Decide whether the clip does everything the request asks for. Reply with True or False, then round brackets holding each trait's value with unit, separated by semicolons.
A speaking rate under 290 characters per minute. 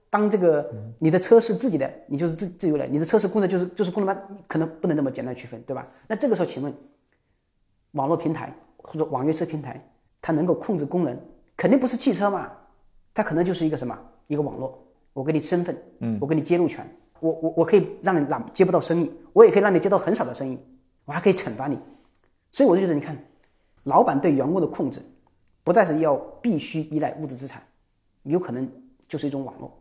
False (340 characters per minute)